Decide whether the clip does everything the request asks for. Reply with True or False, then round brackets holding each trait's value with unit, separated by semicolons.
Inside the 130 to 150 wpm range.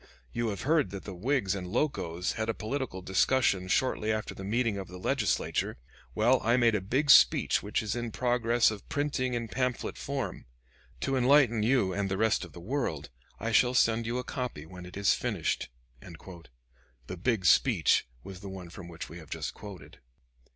False (190 wpm)